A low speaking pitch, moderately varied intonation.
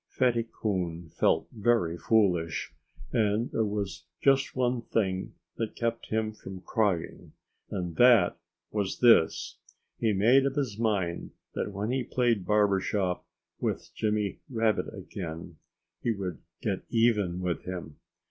Yes: low, 105 Hz; average, 4.0 semitones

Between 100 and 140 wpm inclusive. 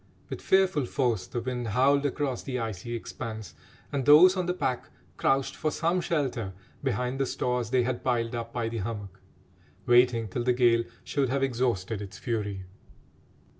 No: average, 170 wpm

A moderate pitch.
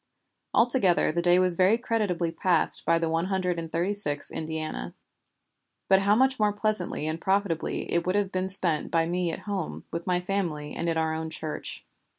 Yes: medium, 180 Hz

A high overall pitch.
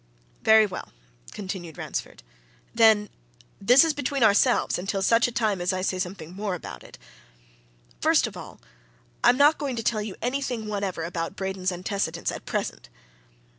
Yes: high, 205 Hz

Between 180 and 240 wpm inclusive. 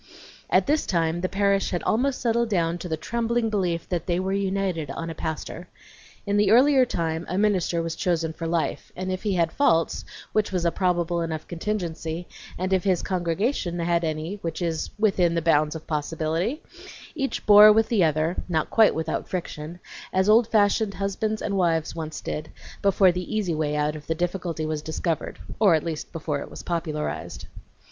Yes: average, 190 wpm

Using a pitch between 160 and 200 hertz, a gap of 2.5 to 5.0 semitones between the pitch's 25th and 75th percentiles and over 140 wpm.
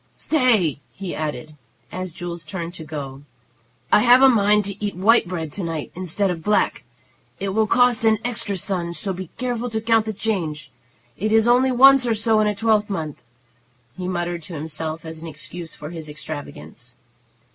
No: medium, 185 Hz; wide, 5.5 semitones; average, 180 wpm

